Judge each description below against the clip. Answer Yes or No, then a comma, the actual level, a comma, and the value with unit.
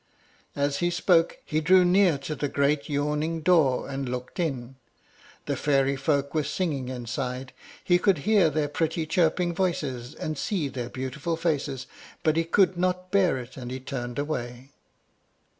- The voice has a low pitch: No, medium, 150 Hz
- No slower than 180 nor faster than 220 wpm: No, average, 160 wpm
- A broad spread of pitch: No, average, 4.3 semitones